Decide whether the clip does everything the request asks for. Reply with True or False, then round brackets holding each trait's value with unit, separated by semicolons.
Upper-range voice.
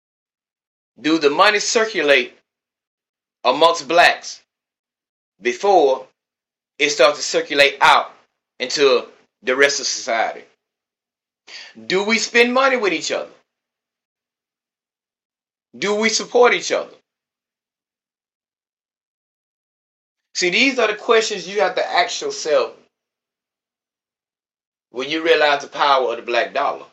True (220 Hz)